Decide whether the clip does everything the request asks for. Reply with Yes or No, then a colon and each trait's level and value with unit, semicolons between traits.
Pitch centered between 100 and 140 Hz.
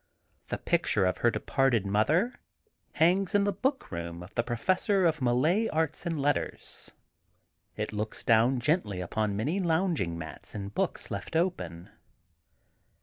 Yes: low, 135 Hz